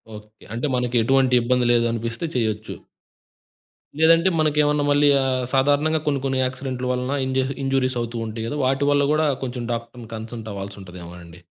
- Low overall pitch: Yes, low, 125 Hz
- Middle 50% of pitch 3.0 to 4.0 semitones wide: Yes, average, 3.5 semitones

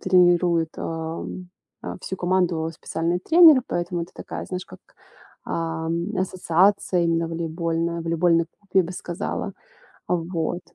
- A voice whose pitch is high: No, medium, 170 Hz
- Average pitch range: No, narrow, 1.7 semitones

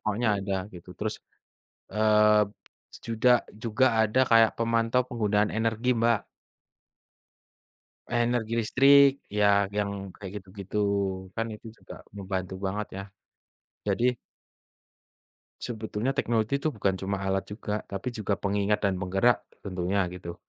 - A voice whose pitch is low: Yes, low, 105 Hz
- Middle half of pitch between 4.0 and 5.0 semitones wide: No, average, 2.7 semitones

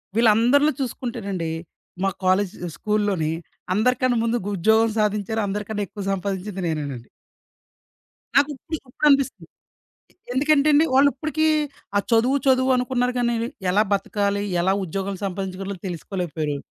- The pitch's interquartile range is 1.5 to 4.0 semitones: No, average, 4.7 semitones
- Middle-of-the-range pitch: No, high, 210 Hz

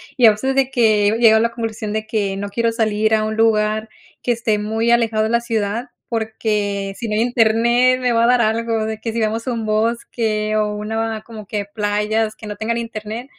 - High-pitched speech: Yes, high, 220 Hz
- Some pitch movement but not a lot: No, narrow, 1.5 semitones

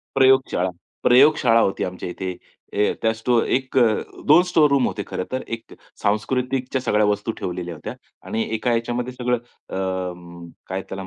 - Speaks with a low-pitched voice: Yes, low, 115 Hz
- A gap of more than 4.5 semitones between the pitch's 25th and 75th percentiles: Yes, average, 5.1 semitones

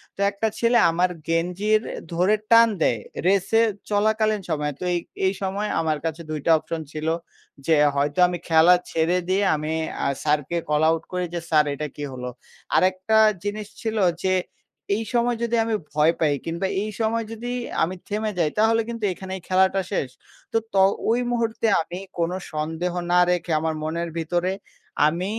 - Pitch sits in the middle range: Yes, medium, 180 Hz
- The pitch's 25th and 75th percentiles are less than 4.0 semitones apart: No, average, 4.9 semitones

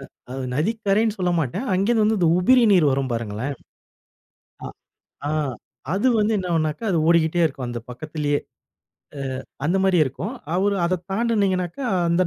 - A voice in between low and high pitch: Yes, medium, 175 Hz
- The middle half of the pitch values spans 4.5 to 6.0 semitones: Yes, average, 5.1 semitones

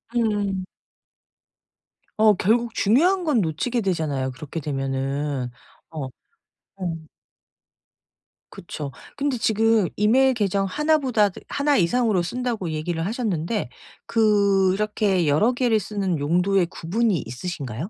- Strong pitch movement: Yes, wide, 6.0 semitones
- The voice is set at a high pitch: Yes, high, 200 Hz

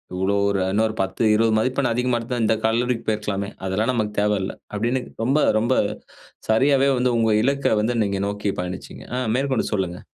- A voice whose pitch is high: No, low, 110 Hz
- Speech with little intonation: No, average, 3.4 semitones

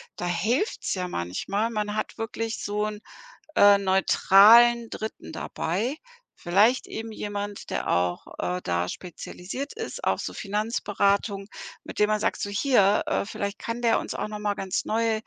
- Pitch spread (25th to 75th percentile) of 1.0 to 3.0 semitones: Yes, narrow, 2.5 semitones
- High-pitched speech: Yes, high, 210 Hz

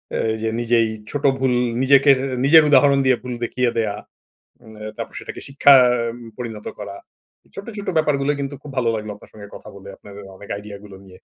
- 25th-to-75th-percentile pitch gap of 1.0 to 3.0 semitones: No, average, 4.8 semitones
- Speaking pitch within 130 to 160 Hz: No, low, 120 Hz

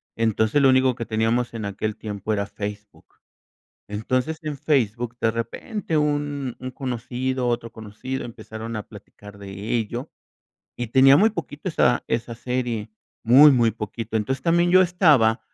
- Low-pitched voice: Yes, low, 120 Hz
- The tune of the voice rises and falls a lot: No, average, 3.5 semitones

